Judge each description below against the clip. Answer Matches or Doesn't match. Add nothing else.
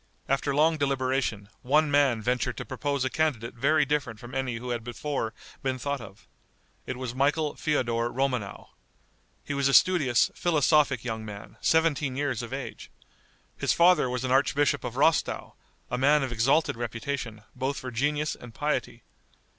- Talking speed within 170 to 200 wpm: Doesn't match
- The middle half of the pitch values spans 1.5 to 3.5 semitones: Matches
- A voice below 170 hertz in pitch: Matches